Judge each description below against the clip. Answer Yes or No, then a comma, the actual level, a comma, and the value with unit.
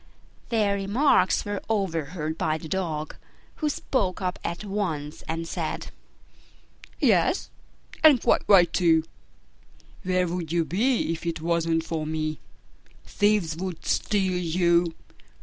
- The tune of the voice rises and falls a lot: No, average, 3.6 semitones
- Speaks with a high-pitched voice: No, medium, 175 Hz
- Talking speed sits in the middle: No, slow, 125 wpm